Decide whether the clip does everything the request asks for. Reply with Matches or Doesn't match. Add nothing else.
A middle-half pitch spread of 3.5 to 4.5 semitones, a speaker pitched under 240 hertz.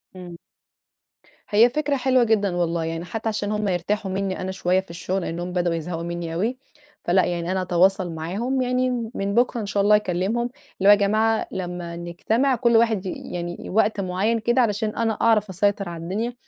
Matches